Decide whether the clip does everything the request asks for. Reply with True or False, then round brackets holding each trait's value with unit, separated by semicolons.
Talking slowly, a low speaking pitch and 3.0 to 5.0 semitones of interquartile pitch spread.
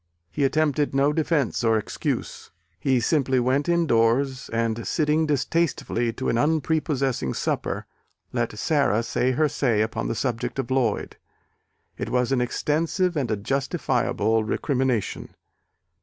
True (130 wpm; 130 Hz; 4.3 semitones)